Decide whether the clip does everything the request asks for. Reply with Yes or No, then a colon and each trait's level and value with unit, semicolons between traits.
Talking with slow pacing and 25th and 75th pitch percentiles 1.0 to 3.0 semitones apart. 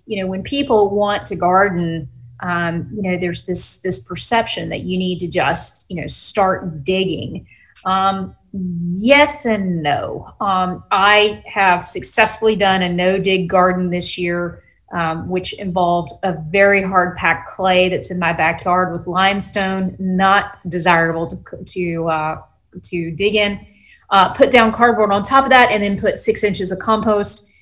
No: average, 165 wpm; narrow, 2.4 semitones